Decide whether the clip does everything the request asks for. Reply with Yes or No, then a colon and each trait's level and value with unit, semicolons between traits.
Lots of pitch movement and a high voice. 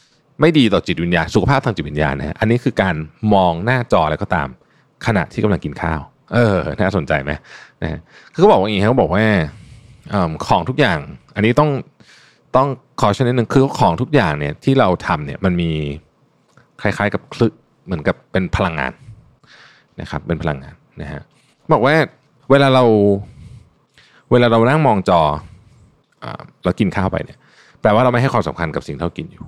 No: wide, 7.7 semitones; low, 105 Hz